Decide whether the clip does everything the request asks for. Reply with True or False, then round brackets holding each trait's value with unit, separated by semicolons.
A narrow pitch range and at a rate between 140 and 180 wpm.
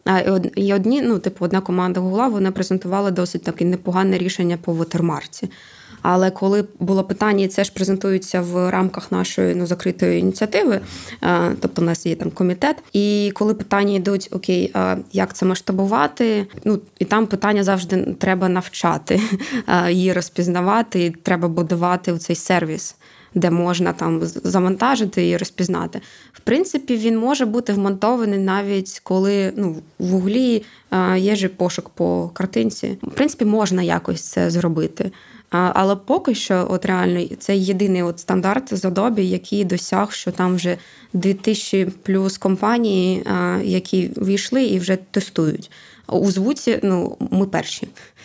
True (2.0 semitones; 145 wpm)